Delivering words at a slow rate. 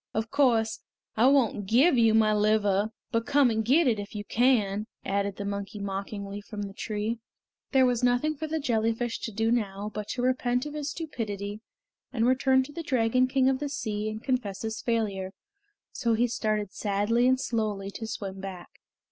No: average, 190 wpm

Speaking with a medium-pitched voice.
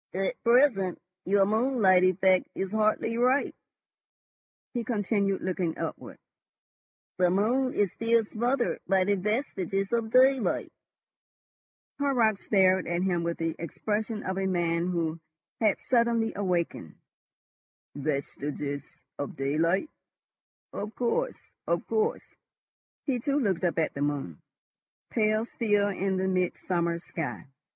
No: high, 195 Hz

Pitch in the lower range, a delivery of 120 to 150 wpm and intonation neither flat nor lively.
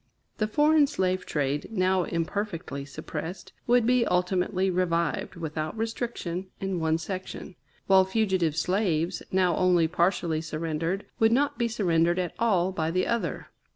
No: medium, 185 Hz; average, 140 wpm; average, 3.9 semitones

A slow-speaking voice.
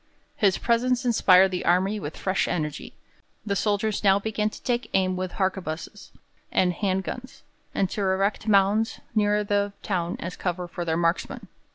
No: average, 165 wpm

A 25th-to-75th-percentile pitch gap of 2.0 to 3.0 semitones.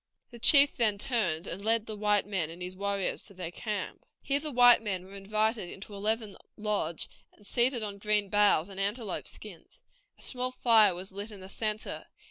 Yes: narrow, 2.6 semitones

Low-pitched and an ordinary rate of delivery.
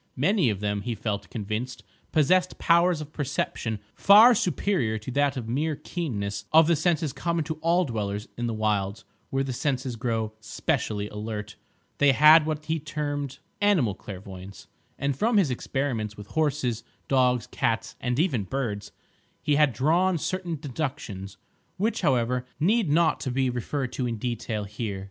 Yes: low, 130 Hz; average, 155 wpm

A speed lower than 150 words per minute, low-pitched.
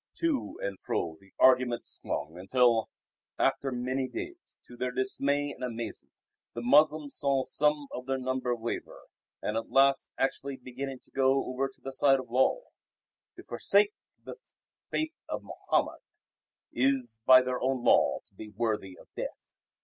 No: average, 155 wpm; low, 130 Hz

